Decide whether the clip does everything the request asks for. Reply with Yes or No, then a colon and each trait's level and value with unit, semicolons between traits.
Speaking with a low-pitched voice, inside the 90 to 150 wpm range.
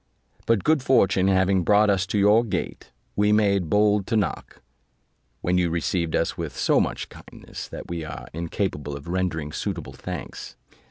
No: very low, 95 Hz; average, 165 wpm